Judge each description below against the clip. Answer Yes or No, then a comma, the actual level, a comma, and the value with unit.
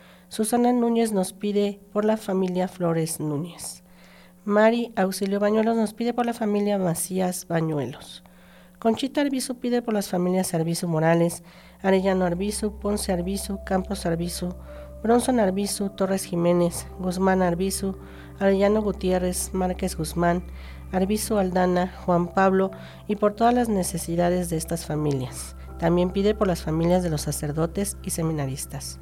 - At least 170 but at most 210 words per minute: No, average, 135 wpm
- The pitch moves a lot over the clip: No, average, 3.4 semitones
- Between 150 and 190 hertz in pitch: Yes, medium, 185 Hz